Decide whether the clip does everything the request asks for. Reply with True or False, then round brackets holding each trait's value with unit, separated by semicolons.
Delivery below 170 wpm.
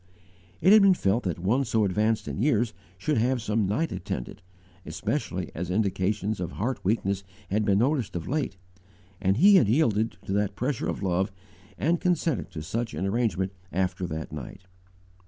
False (175 wpm)